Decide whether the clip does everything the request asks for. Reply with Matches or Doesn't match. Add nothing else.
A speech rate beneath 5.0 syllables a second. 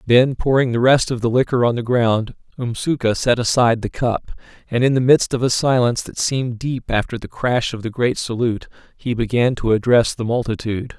Doesn't match